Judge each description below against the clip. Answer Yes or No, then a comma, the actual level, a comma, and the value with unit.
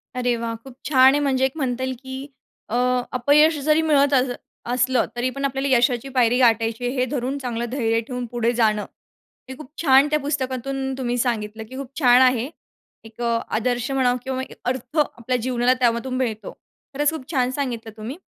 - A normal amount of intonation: No, narrow, 2.0 semitones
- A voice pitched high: Yes, very high, 255 Hz